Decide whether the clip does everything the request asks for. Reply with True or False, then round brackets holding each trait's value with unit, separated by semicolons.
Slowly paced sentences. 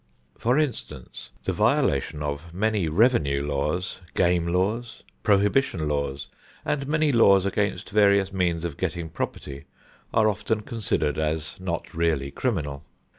True (125 wpm)